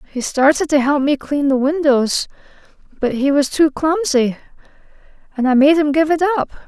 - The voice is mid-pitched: No, very high, 290 Hz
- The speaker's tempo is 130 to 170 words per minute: No, average, 180 wpm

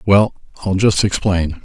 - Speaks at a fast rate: No, average, 145 wpm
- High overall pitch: No, very low, 95 Hz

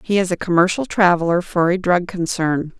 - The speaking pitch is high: No, medium, 180 Hz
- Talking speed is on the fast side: No, average, 195 wpm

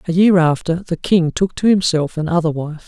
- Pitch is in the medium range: Yes, medium, 170 Hz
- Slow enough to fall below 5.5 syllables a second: Yes, 5.2 syllables/s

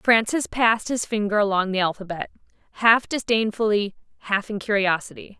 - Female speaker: Yes, female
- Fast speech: No, slow, 135 wpm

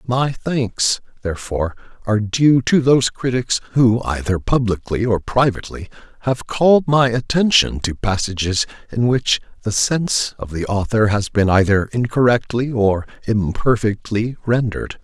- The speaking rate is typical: No, slow, 130 wpm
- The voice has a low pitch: Yes, low, 115 Hz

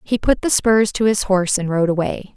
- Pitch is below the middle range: No, high, 200 Hz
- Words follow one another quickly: Yes, fast, 255 wpm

